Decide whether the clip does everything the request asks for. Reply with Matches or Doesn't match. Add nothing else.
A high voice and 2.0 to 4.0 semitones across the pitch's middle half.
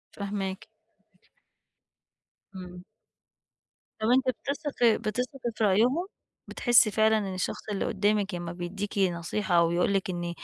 Matches